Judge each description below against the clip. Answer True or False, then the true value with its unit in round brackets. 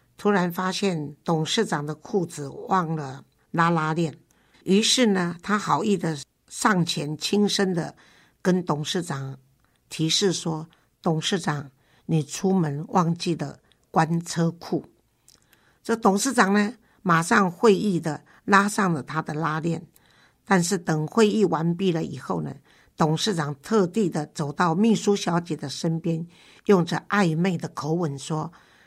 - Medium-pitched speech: True (170 Hz)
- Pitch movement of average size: True (4.0 semitones)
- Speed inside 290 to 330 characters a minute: False (200 characters per minute)